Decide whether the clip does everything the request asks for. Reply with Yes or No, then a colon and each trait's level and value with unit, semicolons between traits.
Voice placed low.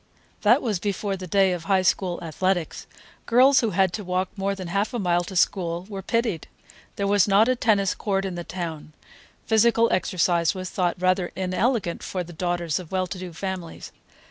No: medium, 185 Hz